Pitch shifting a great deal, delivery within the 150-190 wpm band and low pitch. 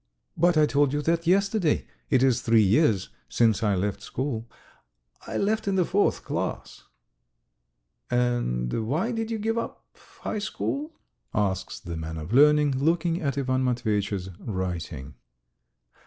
No: wide, 8.7 semitones; average, 140 wpm; low, 130 Hz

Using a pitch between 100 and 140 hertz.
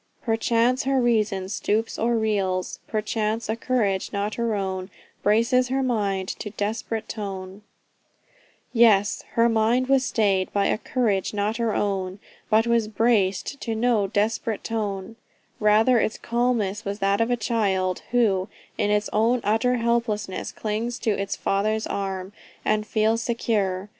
No: high, 215 Hz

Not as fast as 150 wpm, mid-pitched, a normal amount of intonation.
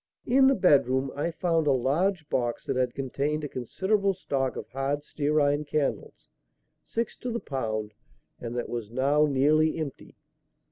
No: average, 155 wpm; medium, 145 Hz; average, 3.5 semitones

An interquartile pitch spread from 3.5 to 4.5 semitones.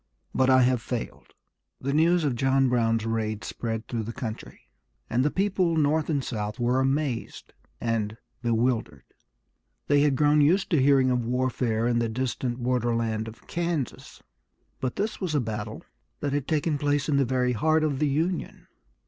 Yes: average, 4.0 semitones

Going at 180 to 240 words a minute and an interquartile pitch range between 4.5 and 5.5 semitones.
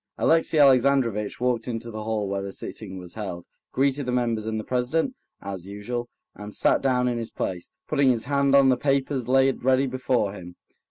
No: average, 195 wpm; average, 4.0 semitones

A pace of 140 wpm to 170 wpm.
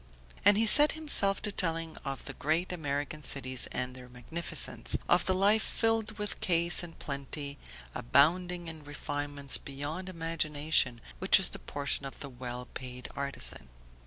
Yes: average, 155 wpm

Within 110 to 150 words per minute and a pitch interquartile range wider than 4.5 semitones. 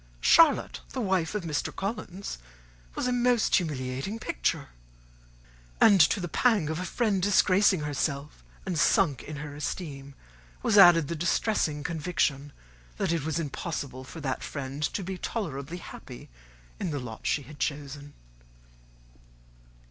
Yes: average, 140 wpm; average, 5.1 semitones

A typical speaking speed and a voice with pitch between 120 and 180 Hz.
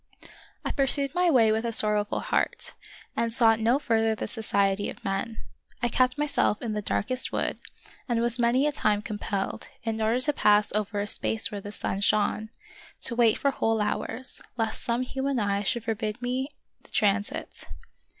No: average, 180 wpm; high, 225 Hz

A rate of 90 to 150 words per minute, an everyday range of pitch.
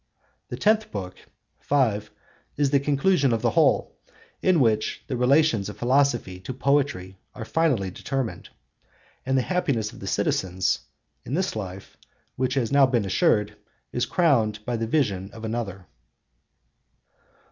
Yes: average, 145 wpm; average, 5.0 semitones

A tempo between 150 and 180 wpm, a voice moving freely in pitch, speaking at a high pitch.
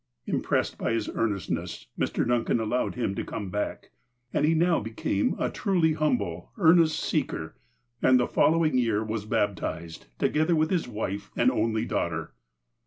No: average, 160 wpm; wide, 7.2 semitones; low, 115 Hz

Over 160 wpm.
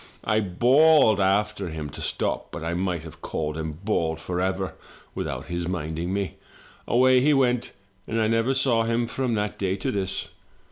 Yes: average, 175 wpm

